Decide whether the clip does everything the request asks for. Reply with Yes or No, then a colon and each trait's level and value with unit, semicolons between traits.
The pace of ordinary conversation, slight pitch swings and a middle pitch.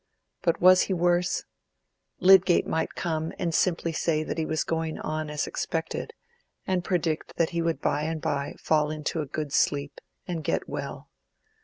Yes: average, 175 wpm; narrow, 2.0 semitones; medium, 160 Hz